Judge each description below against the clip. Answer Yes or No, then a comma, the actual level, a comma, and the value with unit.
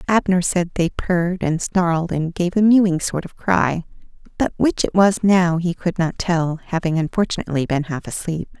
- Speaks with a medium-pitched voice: Yes, medium, 175 Hz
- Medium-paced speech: Yes, average, 190 wpm